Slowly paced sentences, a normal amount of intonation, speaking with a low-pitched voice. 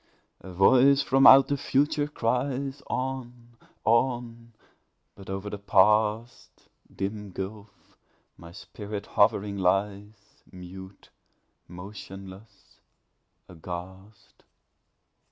Yes: slow, 85 wpm; average, 4.2 semitones; low, 105 Hz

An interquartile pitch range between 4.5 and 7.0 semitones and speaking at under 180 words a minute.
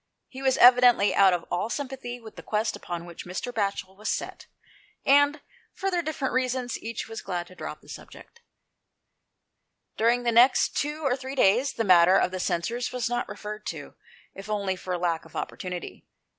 No: wide, 5.5 semitones; average, 185 wpm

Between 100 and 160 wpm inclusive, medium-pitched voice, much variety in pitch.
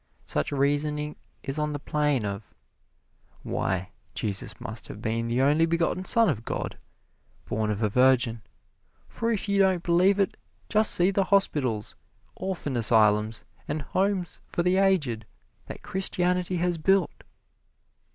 Yes: average, 140 wpm; medium, 150 Hz; wide, 8.1 semitones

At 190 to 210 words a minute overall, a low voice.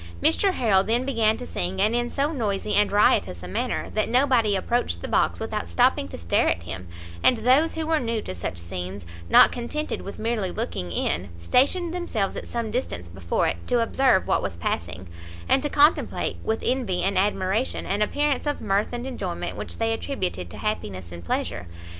No: average, 195 wpm; high, 210 Hz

